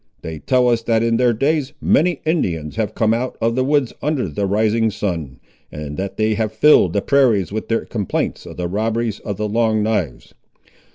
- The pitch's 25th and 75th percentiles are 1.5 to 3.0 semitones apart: No, average, 3.8 semitones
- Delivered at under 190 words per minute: No, average, 195 wpm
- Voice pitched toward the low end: Yes, low, 110 Hz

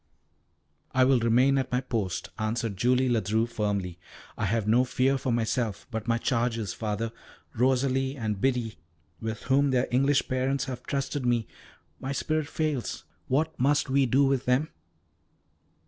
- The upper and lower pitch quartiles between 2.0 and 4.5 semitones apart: Yes, average, 3.0 semitones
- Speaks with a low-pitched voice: Yes, low, 125 Hz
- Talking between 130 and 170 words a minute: Yes, average, 150 wpm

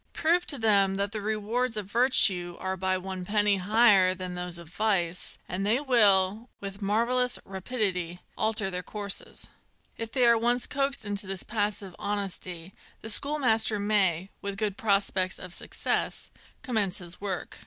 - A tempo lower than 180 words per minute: Yes, average, 155 wpm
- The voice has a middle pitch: No, high, 205 Hz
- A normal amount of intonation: Yes, average, 3.0 semitones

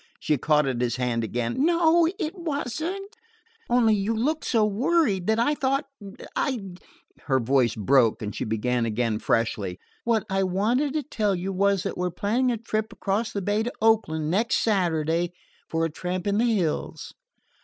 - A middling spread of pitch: No, wide, 7.9 semitones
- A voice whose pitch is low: No, high, 200 Hz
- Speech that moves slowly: No, average, 175 wpm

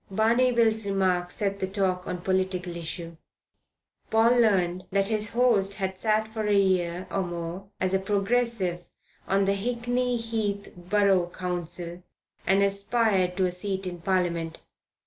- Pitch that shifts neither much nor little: Yes, average, 3.2 semitones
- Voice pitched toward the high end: Yes, high, 195 Hz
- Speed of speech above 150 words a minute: No, average, 145 wpm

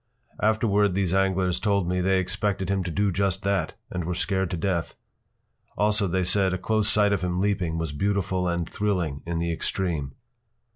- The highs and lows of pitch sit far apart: No, narrow, 2.4 semitones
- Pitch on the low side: Yes, very low, 95 Hz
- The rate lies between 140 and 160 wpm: No, average, 185 wpm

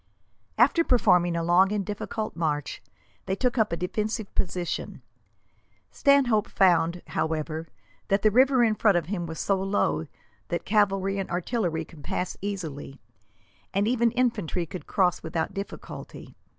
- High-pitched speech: Yes, high, 195 Hz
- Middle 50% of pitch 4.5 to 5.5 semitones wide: No, average, 4.1 semitones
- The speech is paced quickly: No, average, 145 wpm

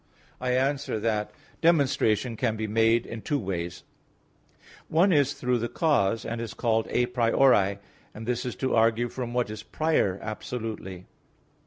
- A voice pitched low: Yes, low, 115 Hz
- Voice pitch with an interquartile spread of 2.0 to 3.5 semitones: Yes, average, 2.9 semitones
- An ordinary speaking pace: Yes, average, 155 wpm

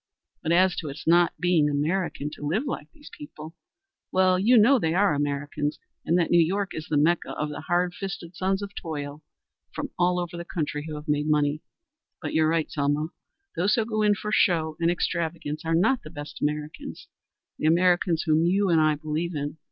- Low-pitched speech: No, medium, 165 Hz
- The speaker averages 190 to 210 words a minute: Yes, average, 200 wpm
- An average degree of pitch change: Yes, average, 3.3 semitones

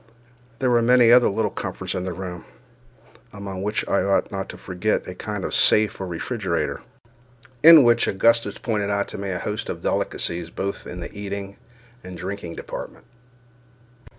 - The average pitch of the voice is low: Yes, low, 100 Hz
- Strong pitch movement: No, average, 3.3 semitones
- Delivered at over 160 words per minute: Yes, average, 170 wpm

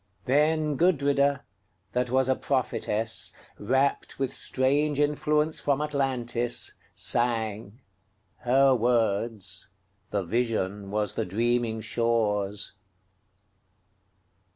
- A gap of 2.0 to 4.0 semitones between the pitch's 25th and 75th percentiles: No, average, 4.4 semitones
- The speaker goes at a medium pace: No, slow, 80 wpm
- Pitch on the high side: No, low, 120 Hz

